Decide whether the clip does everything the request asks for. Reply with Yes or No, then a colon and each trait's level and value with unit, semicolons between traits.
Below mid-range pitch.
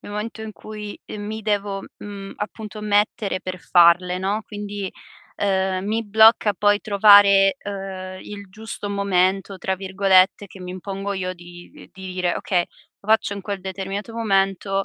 No: high, 200 Hz